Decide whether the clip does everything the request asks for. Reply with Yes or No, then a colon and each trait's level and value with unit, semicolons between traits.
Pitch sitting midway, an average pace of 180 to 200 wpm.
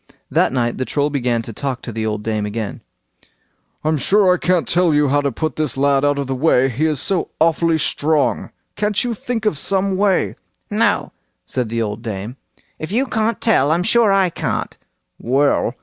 Yes: medium, 145 Hz; average, 190 wpm